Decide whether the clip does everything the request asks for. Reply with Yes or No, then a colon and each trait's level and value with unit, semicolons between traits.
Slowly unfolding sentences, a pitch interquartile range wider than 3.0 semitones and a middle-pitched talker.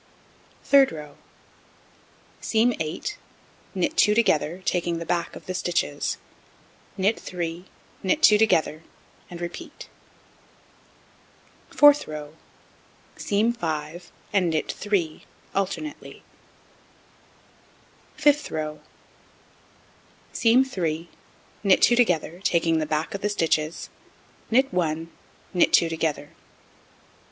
Yes: slow, 100 wpm; average, 4.8 semitones; medium, 175 Hz